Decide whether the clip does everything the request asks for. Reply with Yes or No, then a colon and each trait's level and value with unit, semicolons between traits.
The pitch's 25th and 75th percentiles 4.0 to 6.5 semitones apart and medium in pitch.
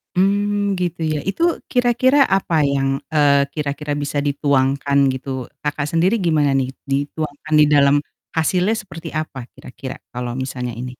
Yes: average, 4.6 semitones; medium, 150 Hz